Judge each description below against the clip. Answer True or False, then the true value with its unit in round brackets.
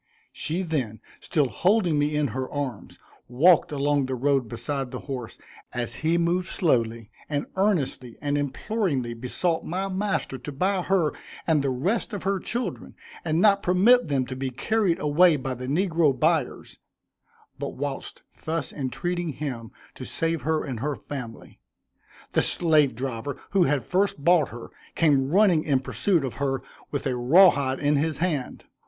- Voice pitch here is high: False (145 Hz)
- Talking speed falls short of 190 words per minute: True (165 wpm)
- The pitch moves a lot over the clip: False (5.0 semitones)